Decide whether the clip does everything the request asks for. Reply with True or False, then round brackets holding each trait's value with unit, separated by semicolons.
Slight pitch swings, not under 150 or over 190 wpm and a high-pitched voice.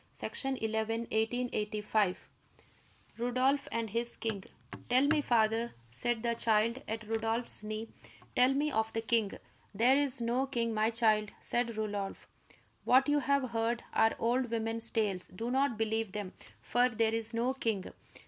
True (2.1 semitones; 160 wpm; 230 Hz)